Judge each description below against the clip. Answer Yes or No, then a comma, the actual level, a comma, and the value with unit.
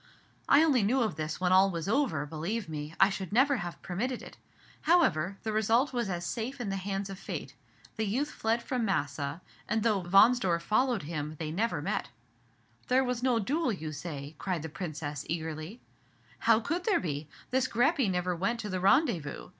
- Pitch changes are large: Yes, wide, 6.6 semitones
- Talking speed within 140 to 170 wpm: No, average, 190 wpm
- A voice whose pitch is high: Yes, high, 195 Hz